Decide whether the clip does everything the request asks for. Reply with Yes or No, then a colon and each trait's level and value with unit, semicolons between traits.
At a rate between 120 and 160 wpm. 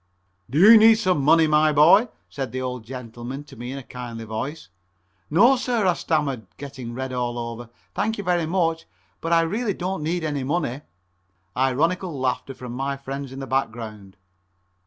No: average, 180 wpm